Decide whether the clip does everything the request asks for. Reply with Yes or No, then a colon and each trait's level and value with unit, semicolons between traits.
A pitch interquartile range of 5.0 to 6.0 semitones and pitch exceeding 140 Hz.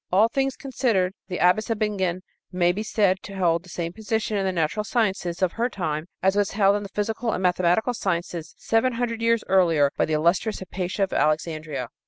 No: average, 4.1 semitones; high, 190 Hz